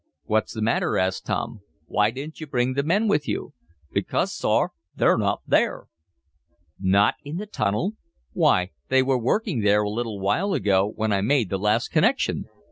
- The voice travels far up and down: Yes, wide, 6.3 semitones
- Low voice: Yes, low, 115 Hz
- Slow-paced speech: No, average, 175 wpm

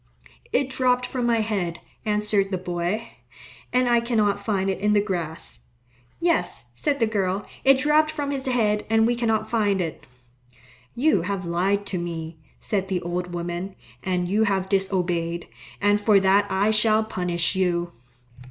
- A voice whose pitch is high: Yes, high, 200 Hz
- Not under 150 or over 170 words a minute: Yes, average, 160 wpm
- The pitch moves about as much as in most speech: Yes, average, 3.8 semitones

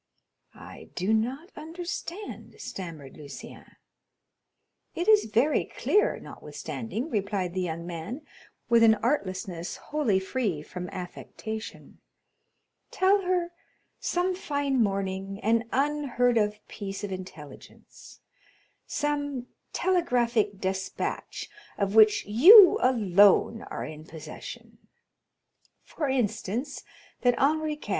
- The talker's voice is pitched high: Yes, high, 225 Hz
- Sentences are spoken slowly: Yes, slow, 100 wpm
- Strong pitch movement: Yes, wide, 7.5 semitones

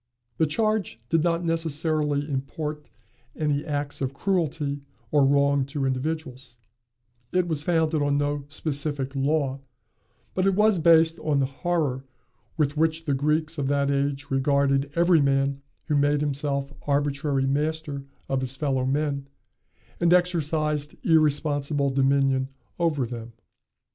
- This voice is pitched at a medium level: Yes, medium, 145 Hz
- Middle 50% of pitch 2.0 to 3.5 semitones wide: Yes, narrow, 2.4 semitones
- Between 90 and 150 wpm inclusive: Yes, slow, 135 wpm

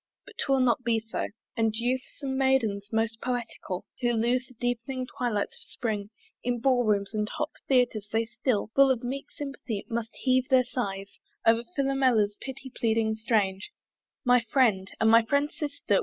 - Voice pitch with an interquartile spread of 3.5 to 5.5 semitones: No, average, 2.8 semitones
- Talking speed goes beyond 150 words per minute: Yes, average, 170 wpm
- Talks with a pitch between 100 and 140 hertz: No, high, 235 Hz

